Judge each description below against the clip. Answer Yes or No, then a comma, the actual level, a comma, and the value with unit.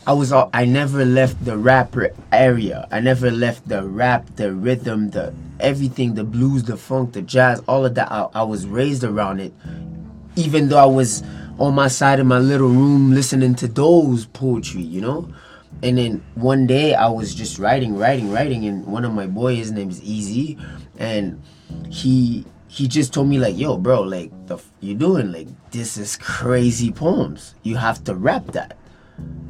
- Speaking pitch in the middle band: No, low, 125 Hz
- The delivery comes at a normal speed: Yes, average, 190 wpm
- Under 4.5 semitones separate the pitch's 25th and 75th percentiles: Yes, average, 3.5 semitones